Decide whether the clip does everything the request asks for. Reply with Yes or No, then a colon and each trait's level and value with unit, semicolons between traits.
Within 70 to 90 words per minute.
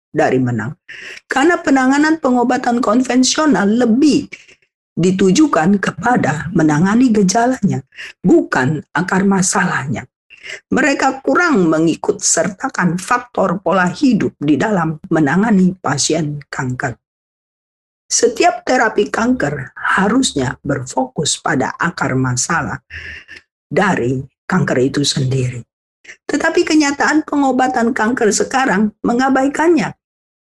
Yes: slow, 85 wpm